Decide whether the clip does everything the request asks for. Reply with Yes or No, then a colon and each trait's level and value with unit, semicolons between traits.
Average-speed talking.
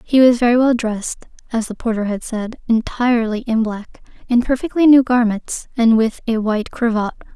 Yes: average, 180 wpm